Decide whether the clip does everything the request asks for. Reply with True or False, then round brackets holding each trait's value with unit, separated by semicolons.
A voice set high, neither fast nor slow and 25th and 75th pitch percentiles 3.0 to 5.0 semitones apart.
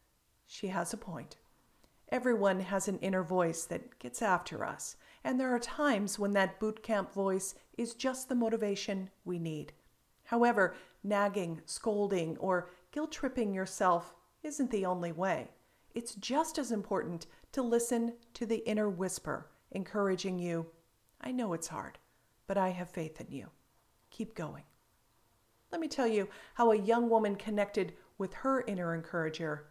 True (200 Hz; 155 wpm; 4.5 semitones)